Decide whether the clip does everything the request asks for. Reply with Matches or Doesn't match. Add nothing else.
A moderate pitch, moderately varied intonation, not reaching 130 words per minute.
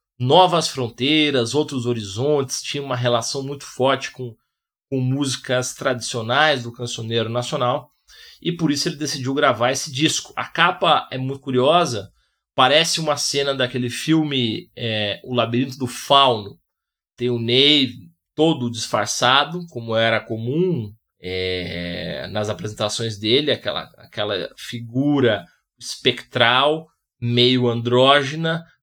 Doesn't match